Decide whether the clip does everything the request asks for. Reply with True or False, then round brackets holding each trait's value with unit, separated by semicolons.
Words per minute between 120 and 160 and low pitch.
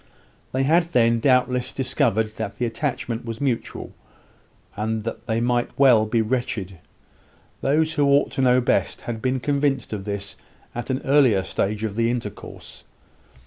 True (150 wpm; 120 Hz)